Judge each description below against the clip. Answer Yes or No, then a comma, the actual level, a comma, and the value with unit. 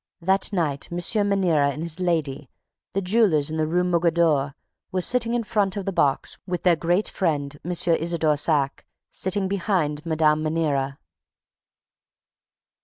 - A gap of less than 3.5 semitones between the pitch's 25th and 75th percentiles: No, average, 3.8 semitones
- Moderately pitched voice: Yes, medium, 170 Hz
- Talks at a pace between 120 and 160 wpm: Yes, average, 150 wpm